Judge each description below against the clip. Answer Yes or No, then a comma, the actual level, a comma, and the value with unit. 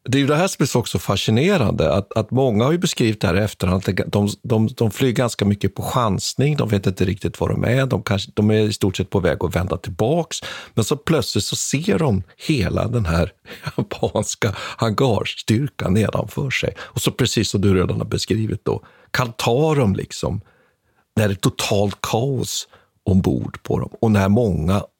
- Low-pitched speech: Yes, low, 110 Hz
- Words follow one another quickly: Yes, fast, 200 wpm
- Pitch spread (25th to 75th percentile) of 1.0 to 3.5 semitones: No, average, 4.5 semitones